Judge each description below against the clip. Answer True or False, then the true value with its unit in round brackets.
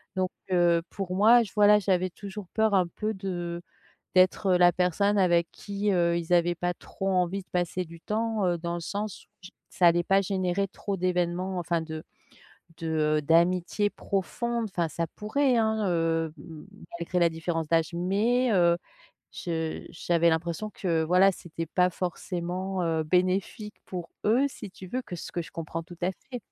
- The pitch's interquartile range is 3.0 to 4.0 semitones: False (2.6 semitones)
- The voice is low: False (180 Hz)